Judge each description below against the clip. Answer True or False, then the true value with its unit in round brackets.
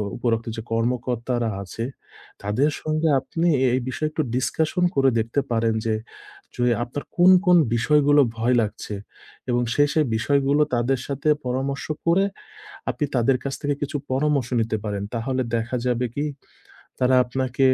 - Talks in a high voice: False (130 Hz)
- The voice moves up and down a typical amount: True (3.7 semitones)